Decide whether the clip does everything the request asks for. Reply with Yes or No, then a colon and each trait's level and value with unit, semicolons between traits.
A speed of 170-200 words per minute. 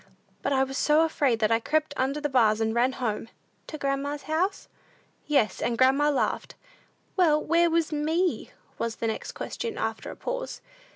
Yes: average, 175 wpm